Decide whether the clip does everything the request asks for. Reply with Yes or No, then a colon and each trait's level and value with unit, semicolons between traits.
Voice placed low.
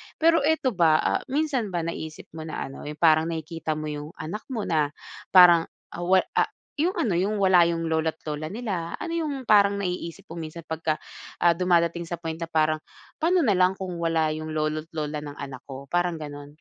No: medium, 170 Hz